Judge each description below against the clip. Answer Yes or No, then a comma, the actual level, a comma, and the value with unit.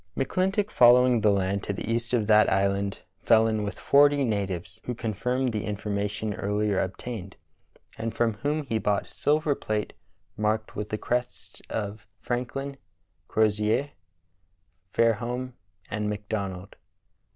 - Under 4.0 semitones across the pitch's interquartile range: Yes, average, 3.2 semitones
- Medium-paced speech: No, slow, 130 wpm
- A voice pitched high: No, low, 110 Hz